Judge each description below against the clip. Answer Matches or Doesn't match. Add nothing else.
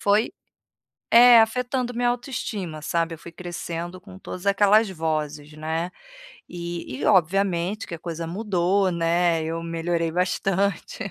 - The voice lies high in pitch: Doesn't match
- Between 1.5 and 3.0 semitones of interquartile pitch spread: Doesn't match